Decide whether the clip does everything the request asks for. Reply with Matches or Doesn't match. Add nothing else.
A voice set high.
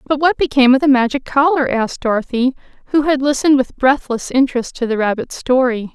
Matches